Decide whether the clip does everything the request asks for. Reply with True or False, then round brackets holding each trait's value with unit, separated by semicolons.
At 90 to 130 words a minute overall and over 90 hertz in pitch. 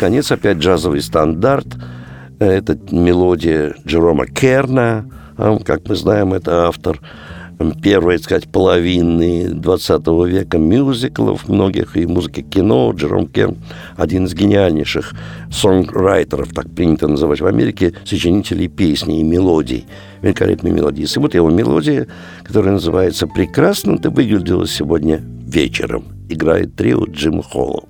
False (120 wpm; 85 Hz)